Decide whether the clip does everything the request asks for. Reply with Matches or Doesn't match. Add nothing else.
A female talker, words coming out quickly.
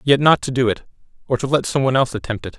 Doesn't match